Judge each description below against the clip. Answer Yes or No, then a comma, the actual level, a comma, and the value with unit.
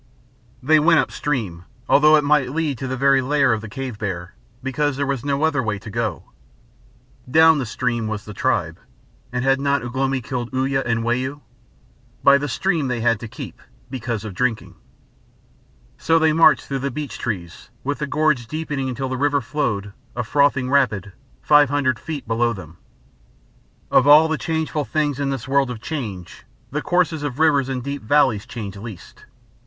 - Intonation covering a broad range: No, average, 3.9 semitones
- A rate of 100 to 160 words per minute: No, average, 180 wpm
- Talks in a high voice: No, low, 135 Hz